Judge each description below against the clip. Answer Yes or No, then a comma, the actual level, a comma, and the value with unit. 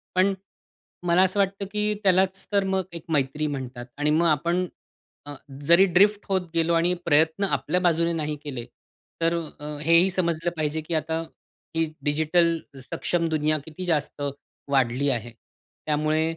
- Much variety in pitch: No, average, 3.2 semitones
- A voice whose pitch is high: No, medium, 165 Hz